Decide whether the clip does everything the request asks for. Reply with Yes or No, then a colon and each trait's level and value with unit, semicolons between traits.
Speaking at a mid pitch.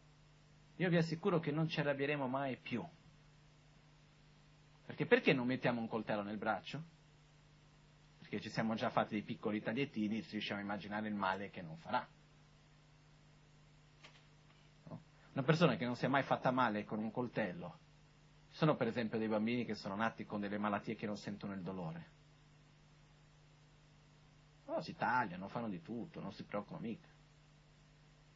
Yes: medium, 150 Hz